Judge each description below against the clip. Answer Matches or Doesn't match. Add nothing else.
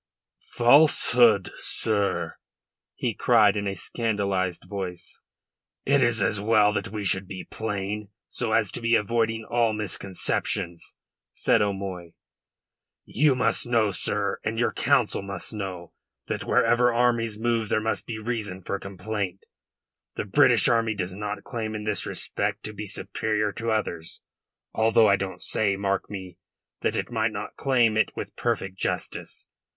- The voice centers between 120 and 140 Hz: Doesn't match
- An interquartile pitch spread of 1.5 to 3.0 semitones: Matches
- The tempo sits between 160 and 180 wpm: Doesn't match